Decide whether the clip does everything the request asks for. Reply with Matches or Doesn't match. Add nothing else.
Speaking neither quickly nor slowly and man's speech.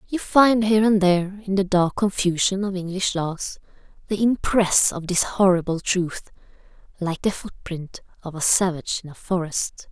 Doesn't match